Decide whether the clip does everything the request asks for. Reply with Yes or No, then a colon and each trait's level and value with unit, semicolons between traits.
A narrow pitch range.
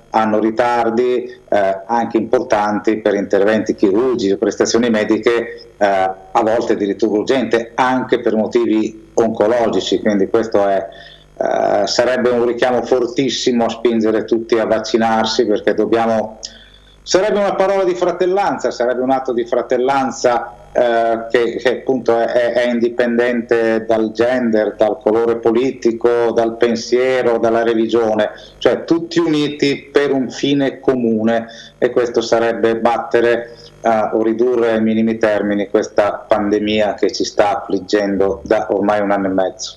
Yes: narrow, 2.0 semitones